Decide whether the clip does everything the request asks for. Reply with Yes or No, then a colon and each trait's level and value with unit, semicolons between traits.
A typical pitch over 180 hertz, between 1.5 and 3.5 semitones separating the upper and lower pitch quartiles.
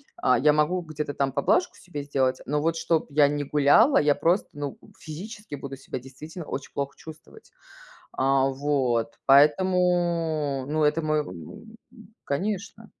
No: medium, 150 Hz; average, 3.1 semitones